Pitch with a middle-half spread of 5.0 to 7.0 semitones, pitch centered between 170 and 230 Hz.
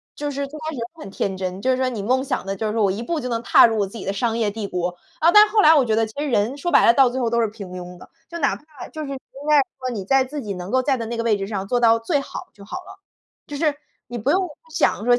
No: wide, 5.6 semitones; high, 240 Hz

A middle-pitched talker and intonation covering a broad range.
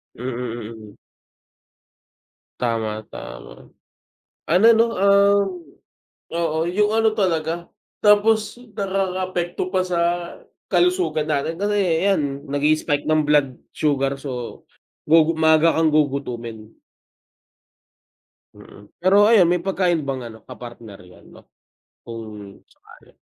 Yes: medium, 160 Hz; wide, 6.9 semitones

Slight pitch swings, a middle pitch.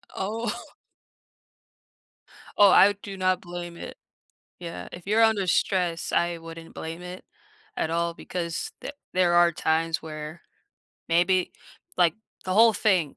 Yes: narrow, 2.2 semitones; medium, 175 Hz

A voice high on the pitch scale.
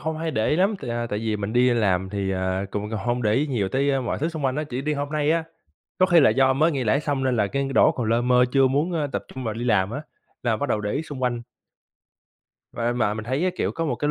No: low, 125 Hz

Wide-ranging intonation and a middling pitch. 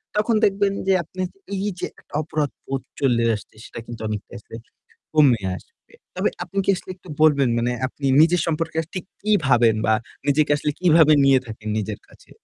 Yes: wide, 6.9 semitones; medium, 150 Hz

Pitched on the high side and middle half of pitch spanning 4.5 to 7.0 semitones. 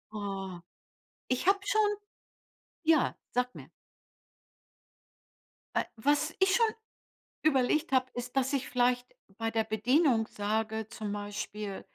Yes: high, 245 Hz; average, 4.9 semitones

